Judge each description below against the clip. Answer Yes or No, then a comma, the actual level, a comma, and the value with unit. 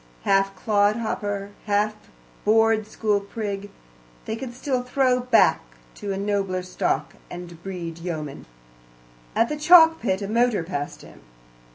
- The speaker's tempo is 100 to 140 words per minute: Yes, slow, 135 wpm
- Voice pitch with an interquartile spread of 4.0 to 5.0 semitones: No, average, 3.3 semitones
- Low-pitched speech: No, high, 205 Hz